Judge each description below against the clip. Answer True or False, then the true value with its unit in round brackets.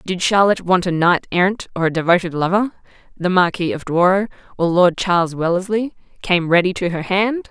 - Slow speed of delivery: False (185 wpm)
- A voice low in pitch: False (185 Hz)